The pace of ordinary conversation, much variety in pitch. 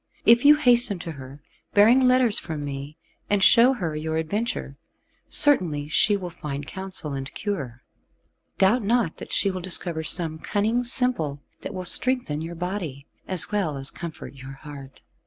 Yes: average, 160 wpm; wide, 6.5 semitones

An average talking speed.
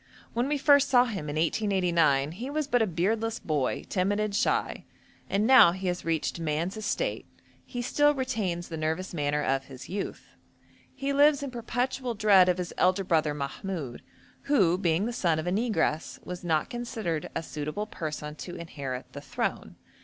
Yes: average, 175 wpm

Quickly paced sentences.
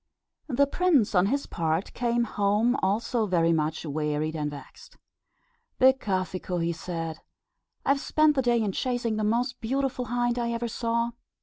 No: average, 160 wpm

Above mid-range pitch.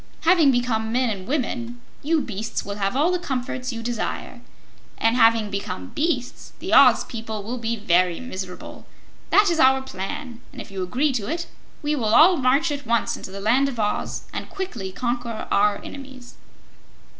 Yes: high, 240 Hz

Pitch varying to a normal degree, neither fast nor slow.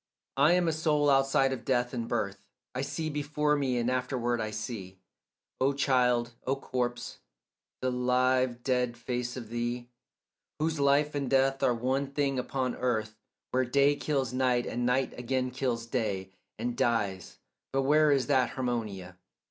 No: narrow, 2.3 semitones; average, 160 wpm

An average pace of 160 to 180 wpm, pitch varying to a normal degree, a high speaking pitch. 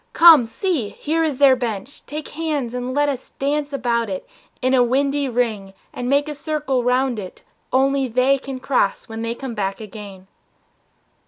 Yes: average, 175 wpm; average, 3.5 semitones; very high, 255 Hz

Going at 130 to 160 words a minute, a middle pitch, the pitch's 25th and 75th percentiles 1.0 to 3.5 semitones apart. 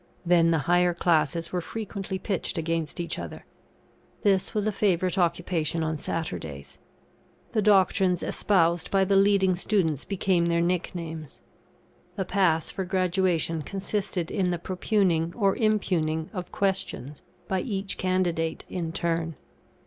Yes: slow, 135 wpm; medium, 180 Hz; average, 2.7 semitones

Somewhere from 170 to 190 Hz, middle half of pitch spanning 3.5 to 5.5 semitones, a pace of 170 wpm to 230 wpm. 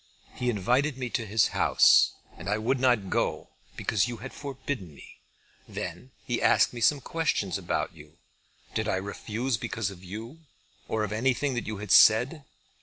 No: low, 115 Hz; average, 3.8 semitones; average, 175 wpm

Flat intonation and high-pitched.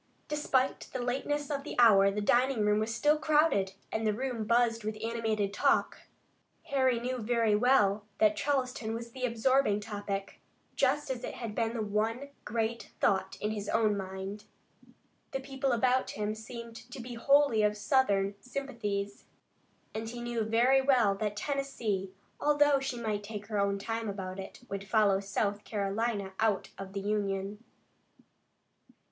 No: average, 3.6 semitones; high, 225 Hz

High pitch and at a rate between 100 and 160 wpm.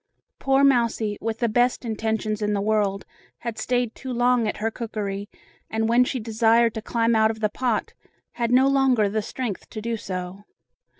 No: high, 225 Hz; average, 185 wpm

